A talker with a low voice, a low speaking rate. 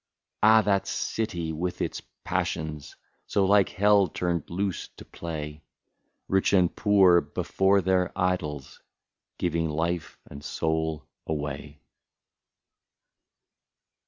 Yes: very low, 85 Hz; slow, 100 wpm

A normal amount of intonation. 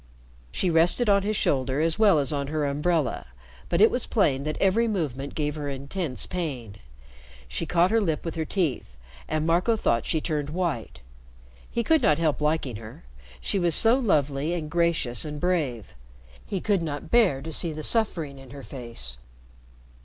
Yes: average, 4.5 semitones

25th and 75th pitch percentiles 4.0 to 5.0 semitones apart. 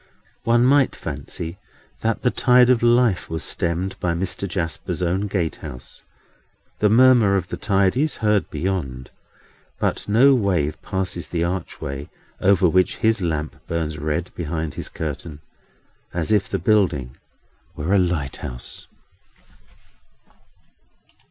Yes: average, 4.7 semitones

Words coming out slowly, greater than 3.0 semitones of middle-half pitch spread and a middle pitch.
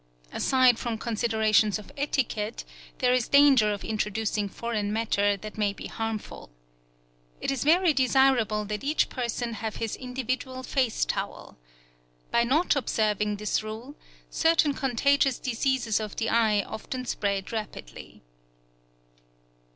No: slow, 130 wpm; average, 3.5 semitones; high, 230 Hz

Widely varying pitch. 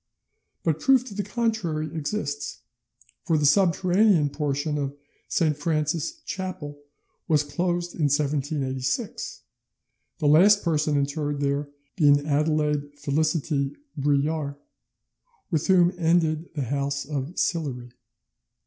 No: average, 3.2 semitones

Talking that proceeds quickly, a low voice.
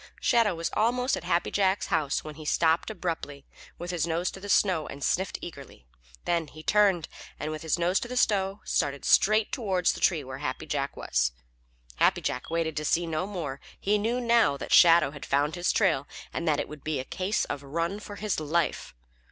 No: fast, 210 wpm; medium, 170 Hz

